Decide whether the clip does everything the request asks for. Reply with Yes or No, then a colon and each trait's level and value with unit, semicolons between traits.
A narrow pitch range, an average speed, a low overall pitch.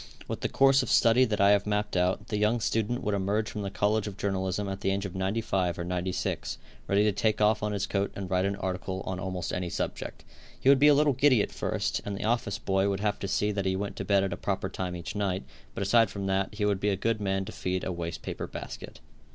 No: narrow, 1.9 semitones; fast, 260 wpm; low, 100 Hz